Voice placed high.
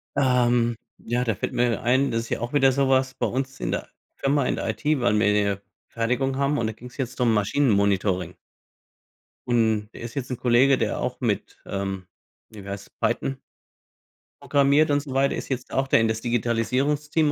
No: low, 120 Hz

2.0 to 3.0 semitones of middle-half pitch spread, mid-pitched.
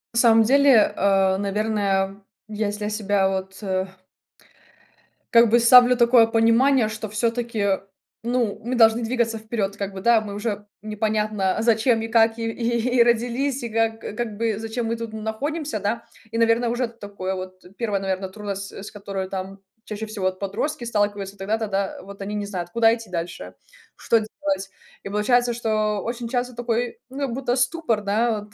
No: average, 2.7 semitones; high, 220 Hz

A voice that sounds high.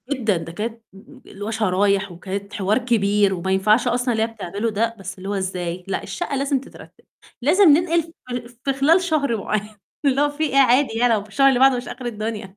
Yes: high, 225 Hz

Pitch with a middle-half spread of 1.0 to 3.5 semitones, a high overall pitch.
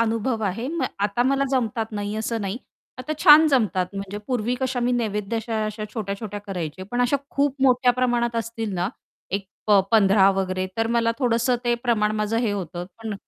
Yes: average, 3.1 semitones; high, 225 Hz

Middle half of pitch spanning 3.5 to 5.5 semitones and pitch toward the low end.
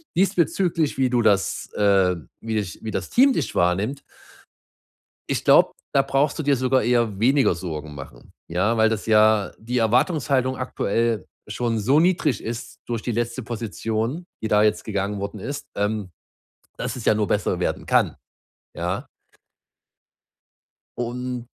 Yes: average, 3.9 semitones; low, 115 Hz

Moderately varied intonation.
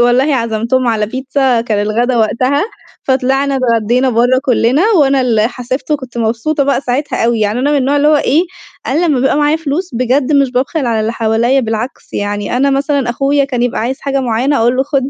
Yes: average, 3.1 semitones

